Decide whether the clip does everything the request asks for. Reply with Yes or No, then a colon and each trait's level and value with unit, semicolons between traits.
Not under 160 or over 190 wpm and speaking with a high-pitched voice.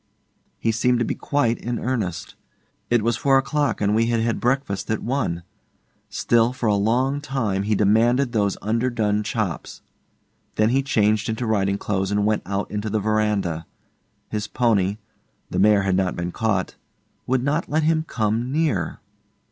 No: average, 165 wpm; low, 110 Hz